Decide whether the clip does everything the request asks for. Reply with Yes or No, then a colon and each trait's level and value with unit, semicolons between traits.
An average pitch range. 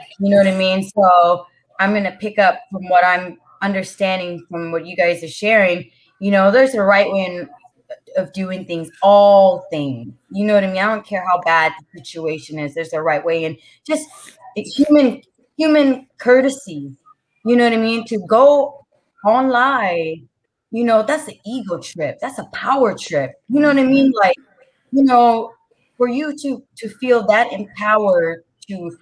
No: wide, 6.6 semitones